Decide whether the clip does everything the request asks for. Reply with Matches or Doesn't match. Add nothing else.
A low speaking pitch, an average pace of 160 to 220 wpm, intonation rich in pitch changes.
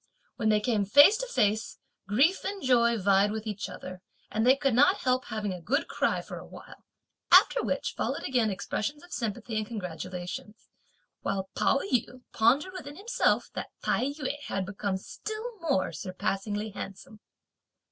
Doesn't match